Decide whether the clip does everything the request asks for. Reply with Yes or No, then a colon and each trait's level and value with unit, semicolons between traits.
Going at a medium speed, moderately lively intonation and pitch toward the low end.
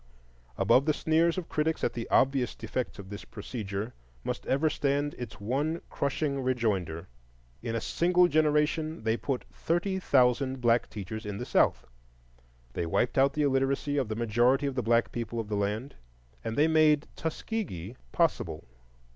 Yes: average, 165 wpm; average, 5.0 semitones; low, 130 Hz